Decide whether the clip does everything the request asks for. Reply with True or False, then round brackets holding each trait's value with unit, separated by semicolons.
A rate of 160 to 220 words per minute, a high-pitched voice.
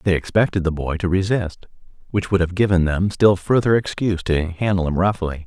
False (200 wpm; 90 Hz)